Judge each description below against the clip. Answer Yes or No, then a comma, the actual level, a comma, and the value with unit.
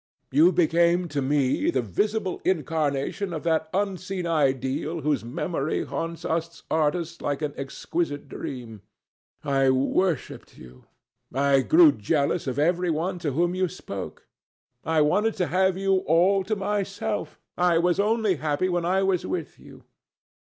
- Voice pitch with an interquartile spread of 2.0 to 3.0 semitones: No, average, 4.4 semitones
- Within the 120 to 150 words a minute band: Yes, average, 145 wpm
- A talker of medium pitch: Yes, medium, 165 Hz